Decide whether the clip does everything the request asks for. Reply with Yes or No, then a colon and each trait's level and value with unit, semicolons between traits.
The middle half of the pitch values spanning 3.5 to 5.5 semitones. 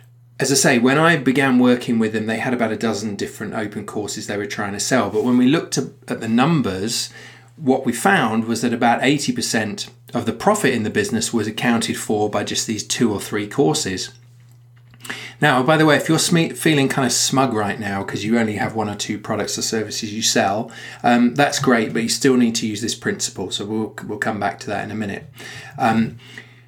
No: average, 2.7 semitones